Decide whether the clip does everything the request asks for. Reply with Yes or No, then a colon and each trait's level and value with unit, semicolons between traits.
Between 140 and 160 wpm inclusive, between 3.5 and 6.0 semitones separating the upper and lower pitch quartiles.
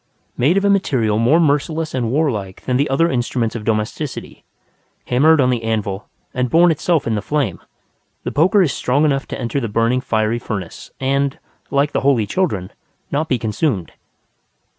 No: average, 175 wpm; average, 5.1 semitones